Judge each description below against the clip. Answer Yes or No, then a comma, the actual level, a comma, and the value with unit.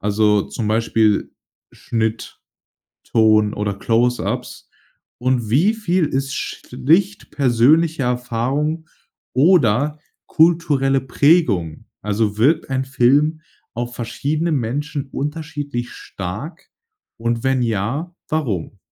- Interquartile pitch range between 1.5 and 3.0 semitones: No, average, 5.2 semitones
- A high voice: No, low, 130 Hz